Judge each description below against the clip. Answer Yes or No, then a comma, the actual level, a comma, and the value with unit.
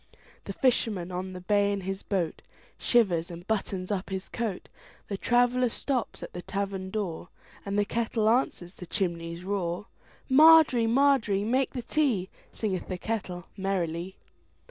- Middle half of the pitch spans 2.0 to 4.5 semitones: Yes, average, 4.2 semitones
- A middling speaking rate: No, slow, 130 wpm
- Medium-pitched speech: No, high, 200 Hz